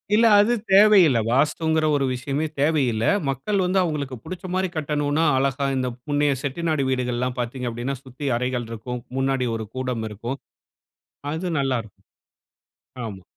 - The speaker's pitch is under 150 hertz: Yes, low, 135 Hz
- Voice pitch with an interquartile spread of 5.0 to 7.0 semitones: No, average, 4.0 semitones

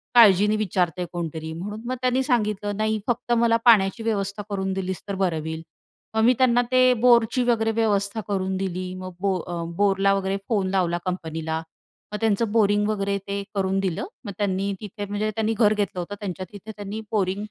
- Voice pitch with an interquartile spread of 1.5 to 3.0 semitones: Yes, narrow, 2.6 semitones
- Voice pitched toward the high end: Yes, high, 200 Hz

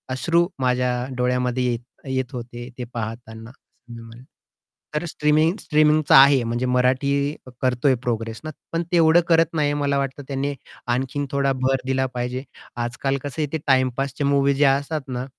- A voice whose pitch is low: Yes, low, 130 Hz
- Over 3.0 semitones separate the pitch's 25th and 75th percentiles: No, narrow, 2.5 semitones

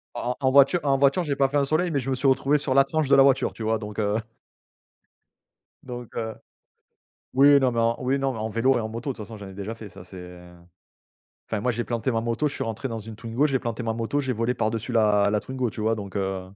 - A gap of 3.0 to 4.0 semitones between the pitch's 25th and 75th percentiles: Yes, average, 3.7 semitones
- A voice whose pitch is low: Yes, low, 115 Hz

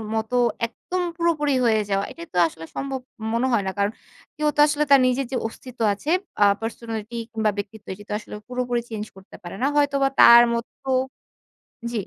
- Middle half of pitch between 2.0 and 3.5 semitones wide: No, average, 4.3 semitones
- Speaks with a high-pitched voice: Yes, high, 235 Hz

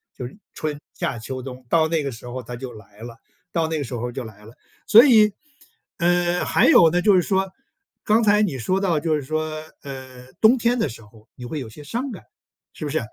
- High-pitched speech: No, medium, 150 Hz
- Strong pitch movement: Yes, wide, 6.4 semitones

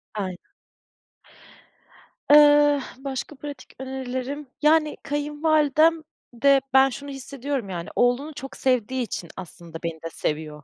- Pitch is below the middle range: No, very high, 270 Hz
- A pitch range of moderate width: Yes, average, 4.1 semitones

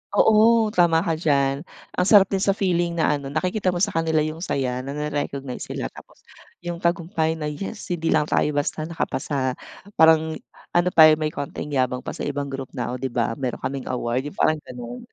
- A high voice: No, medium, 155 Hz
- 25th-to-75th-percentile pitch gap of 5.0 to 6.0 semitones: No, average, 4.0 semitones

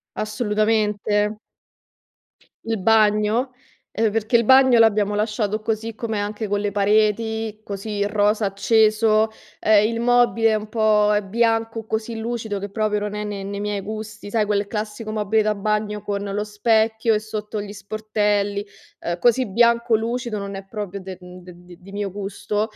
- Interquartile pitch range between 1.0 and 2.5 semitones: Yes, narrow, 1.4 semitones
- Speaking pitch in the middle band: No, high, 215 Hz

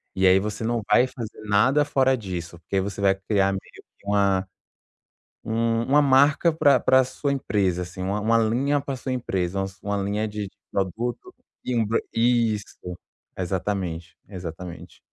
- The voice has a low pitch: Yes, low, 105 Hz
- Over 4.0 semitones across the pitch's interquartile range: Yes, average, 4.4 semitones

